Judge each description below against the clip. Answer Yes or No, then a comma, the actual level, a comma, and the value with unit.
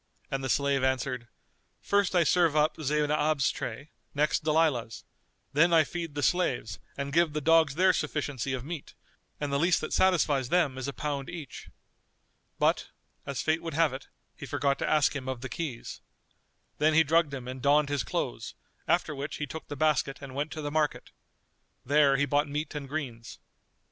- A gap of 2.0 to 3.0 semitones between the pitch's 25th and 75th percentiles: Yes, narrow, 2.5 semitones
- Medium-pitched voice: Yes, medium, 145 Hz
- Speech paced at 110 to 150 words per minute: No, average, 185 wpm